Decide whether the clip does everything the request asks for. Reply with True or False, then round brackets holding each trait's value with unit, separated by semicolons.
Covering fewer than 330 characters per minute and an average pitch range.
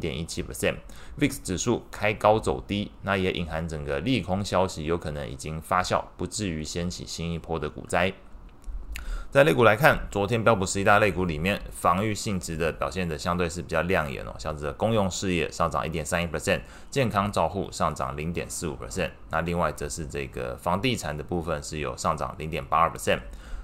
False (360 characters per minute; 3.7 semitones)